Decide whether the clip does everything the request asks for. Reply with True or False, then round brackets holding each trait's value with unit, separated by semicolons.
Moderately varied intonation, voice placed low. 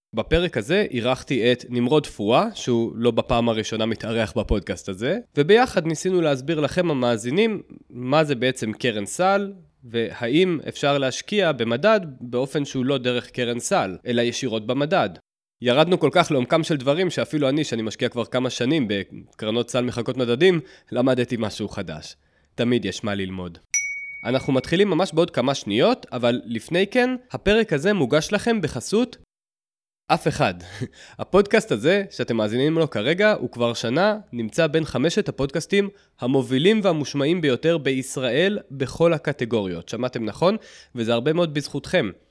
False (6.1 semitones; 130 Hz)